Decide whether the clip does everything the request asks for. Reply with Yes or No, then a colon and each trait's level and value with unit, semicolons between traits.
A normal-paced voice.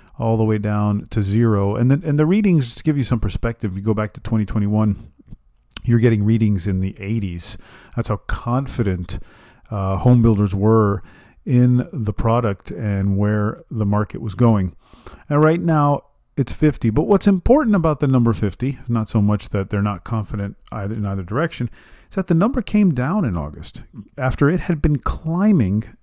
Yes: average, 185 wpm